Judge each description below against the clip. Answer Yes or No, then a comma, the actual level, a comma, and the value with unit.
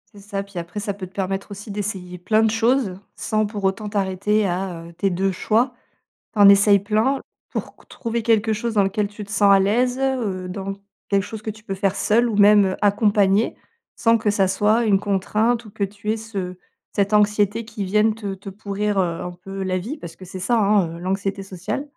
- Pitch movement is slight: Yes, narrow, 2.0 semitones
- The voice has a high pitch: Yes, high, 205 Hz